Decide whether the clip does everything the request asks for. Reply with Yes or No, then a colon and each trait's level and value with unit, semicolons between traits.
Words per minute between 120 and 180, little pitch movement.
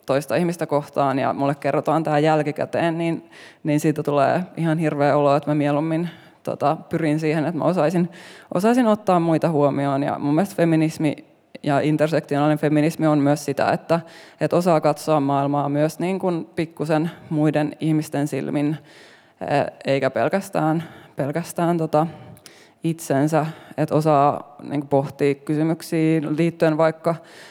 Yes: average, 135 wpm; narrow, 2.1 semitones